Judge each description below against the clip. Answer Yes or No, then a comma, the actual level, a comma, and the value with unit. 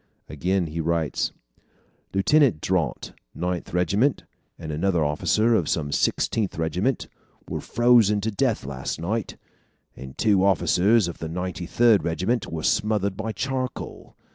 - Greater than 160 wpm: No, slow, 135 wpm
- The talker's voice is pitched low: Yes, very low, 95 Hz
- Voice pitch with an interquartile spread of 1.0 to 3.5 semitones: No, average, 5.2 semitones